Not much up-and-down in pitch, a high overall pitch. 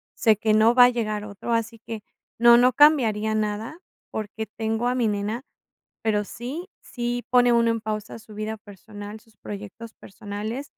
Yes: narrow, 2.1 semitones; high, 220 Hz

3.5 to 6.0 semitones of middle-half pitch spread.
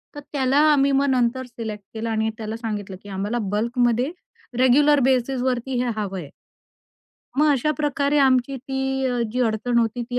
No: average, 3.1 semitones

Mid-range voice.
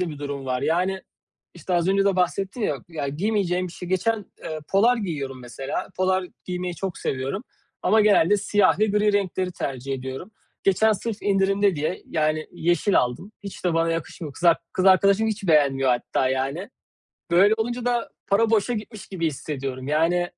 Yes: medium, 180 Hz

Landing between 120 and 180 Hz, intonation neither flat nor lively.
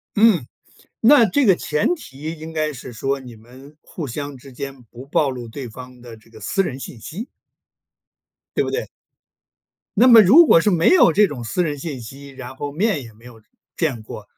No: medium, 140 Hz; wide, 6.0 semitones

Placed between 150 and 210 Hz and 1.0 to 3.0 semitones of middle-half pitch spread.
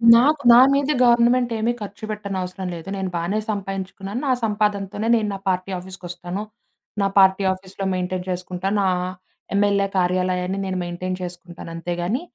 Yes: high, 190 Hz; narrow, 2.4 semitones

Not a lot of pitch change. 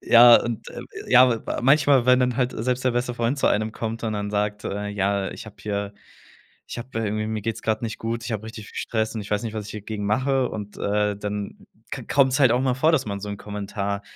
No: average, 3.1 semitones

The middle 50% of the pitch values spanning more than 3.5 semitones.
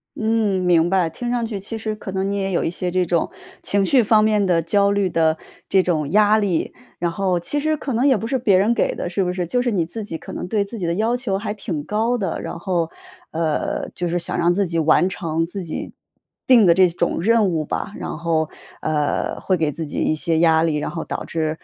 Yes: average, 4.2 semitones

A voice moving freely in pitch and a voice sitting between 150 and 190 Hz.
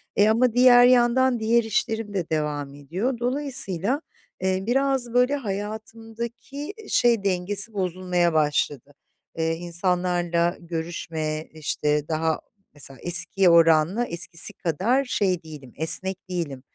Yes: wide, 6.3 semitones; medium, 185 Hz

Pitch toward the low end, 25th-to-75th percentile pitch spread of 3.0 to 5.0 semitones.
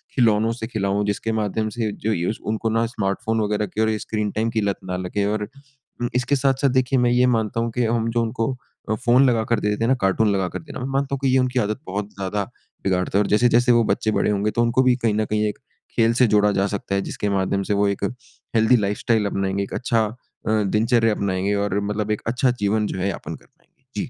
No: low, 110 Hz; narrow, 2.5 semitones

